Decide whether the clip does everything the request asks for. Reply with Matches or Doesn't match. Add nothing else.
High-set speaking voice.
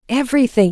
Matches